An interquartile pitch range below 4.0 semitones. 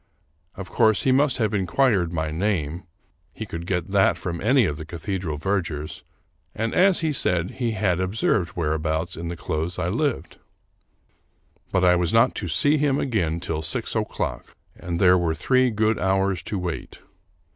No: average, 5.0 semitones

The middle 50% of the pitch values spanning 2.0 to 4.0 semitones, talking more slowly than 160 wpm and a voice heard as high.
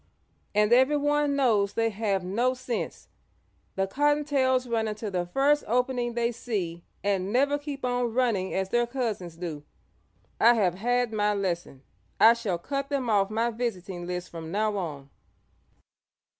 No: average, 4.7 semitones; average, 150 wpm; high, 225 Hz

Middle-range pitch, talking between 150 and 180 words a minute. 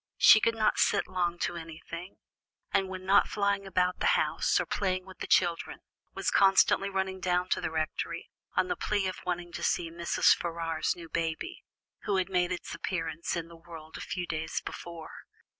No: medium, 180 Hz; average, 190 wpm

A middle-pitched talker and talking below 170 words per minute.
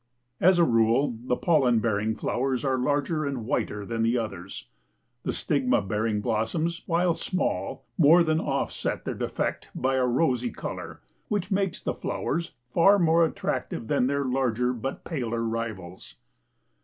No: low, 130 Hz; average, 150 wpm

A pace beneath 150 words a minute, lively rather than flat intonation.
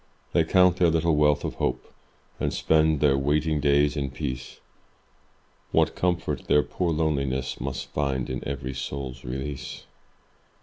No: average, 140 wpm; average, 2.9 semitones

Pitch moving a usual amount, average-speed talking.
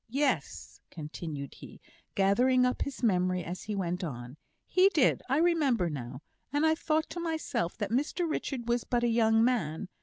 No: wide, 8.4 semitones; average, 175 wpm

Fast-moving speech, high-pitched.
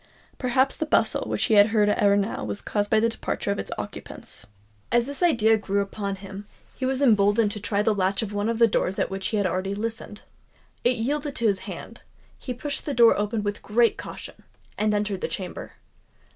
Yes: fast, 215 wpm; high, 210 Hz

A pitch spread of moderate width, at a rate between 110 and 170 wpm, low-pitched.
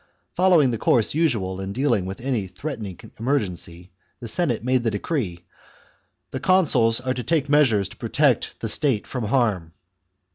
No: wide, 6.1 semitones; average, 160 wpm; low, 120 Hz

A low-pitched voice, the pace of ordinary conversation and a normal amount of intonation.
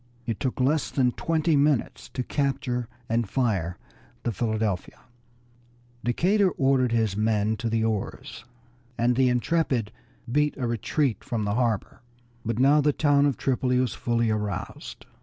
Yes: low, 120 Hz; average, 145 wpm; average, 3.7 semitones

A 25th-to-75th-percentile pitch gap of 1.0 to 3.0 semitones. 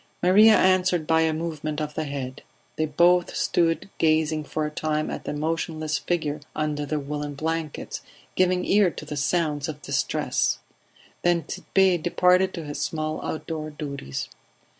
Yes: narrow, 2.6 semitones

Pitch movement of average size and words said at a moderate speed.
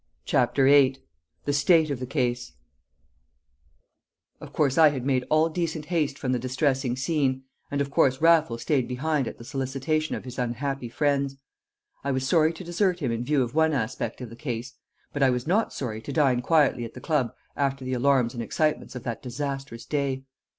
Yes: average, 3.2 semitones; average, 190 wpm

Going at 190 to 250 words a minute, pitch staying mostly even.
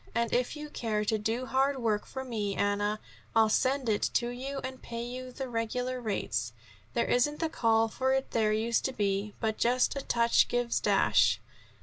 No: average, 195 wpm; average, 3.2 semitones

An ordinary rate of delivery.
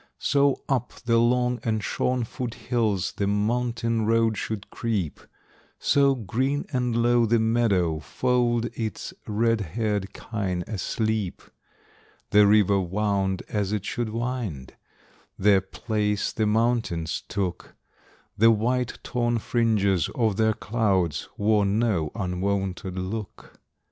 No: slow, 120 wpm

